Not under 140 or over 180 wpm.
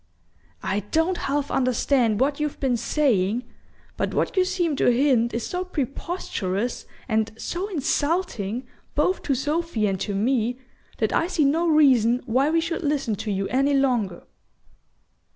Yes: average, 150 wpm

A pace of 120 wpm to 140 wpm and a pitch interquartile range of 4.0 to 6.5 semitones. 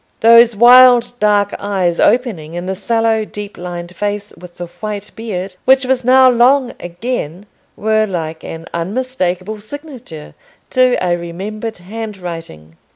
Yes: slow, 135 wpm; average, 5.2 semitones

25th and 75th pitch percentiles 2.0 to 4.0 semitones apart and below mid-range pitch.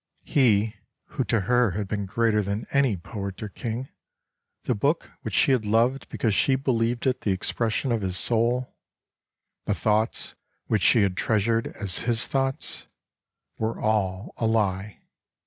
Yes: average, 3.2 semitones; low, 110 Hz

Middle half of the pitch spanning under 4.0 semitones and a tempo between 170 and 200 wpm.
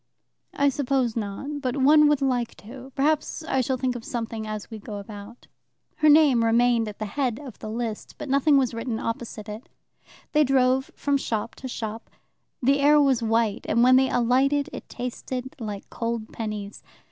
Yes: average, 3.5 semitones; average, 185 wpm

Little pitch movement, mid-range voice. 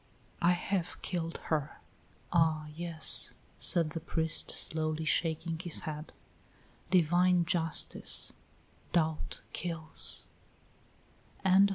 Yes: narrow, 1.6 semitones; medium, 165 Hz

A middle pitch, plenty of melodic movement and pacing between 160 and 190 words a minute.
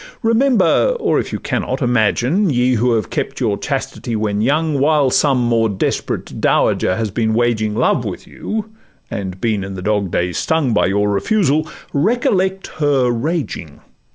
No: low, 120 Hz; wide, 6.8 semitones; average, 165 wpm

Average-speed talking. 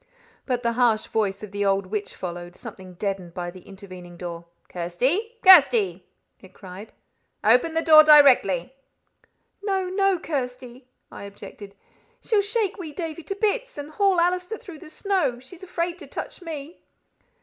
Yes: average, 155 wpm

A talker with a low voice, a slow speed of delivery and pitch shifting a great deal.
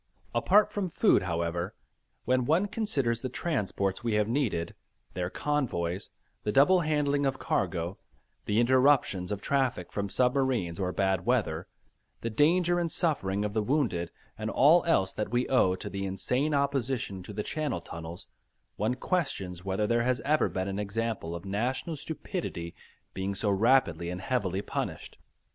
No: low, 115 Hz; average, 155 wpm; wide, 6.6 semitones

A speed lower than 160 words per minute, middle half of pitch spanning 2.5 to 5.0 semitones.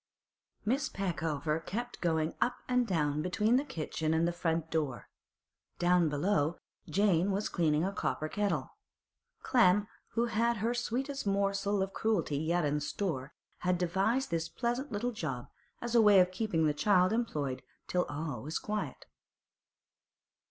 No: average, 150 wpm; wide, 5.4 semitones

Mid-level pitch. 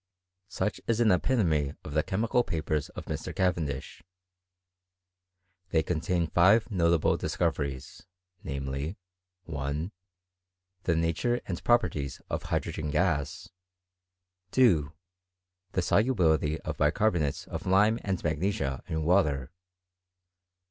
No: very low, 85 Hz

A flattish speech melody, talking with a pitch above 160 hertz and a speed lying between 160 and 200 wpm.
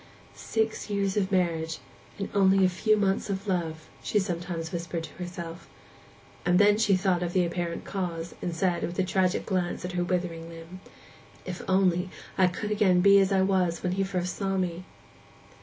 Yes: narrow, 2.0 semitones; medium, 185 Hz; average, 185 wpm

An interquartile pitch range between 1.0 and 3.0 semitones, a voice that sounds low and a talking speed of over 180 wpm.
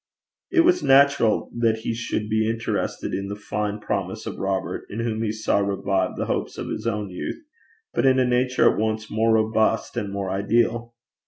Yes: narrow, 2.5 semitones; low, 110 Hz; average, 190 wpm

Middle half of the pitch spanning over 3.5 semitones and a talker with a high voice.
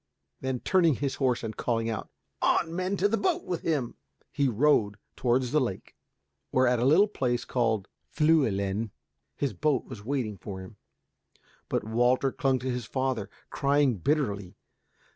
No: average, 4.6 semitones; low, 130 Hz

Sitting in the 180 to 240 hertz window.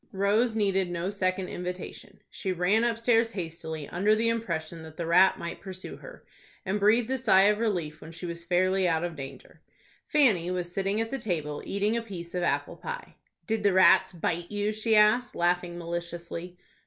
Yes: high, 190 Hz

